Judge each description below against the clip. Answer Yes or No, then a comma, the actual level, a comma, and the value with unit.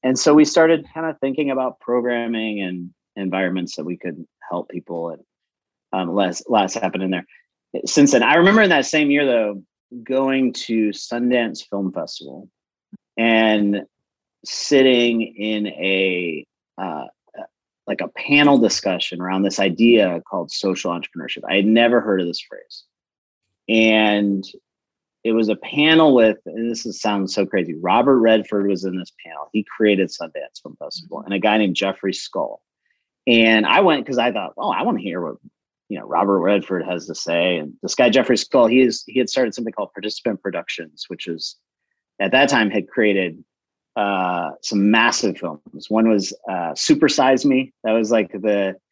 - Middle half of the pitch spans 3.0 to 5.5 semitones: Yes, average, 4.1 semitones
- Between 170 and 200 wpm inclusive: Yes, average, 175 wpm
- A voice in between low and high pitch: No, low, 110 Hz